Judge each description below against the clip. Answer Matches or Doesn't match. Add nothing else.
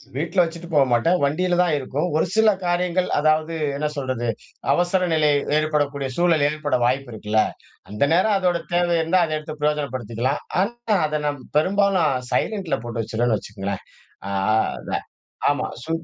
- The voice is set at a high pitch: Doesn't match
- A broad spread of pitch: Doesn't match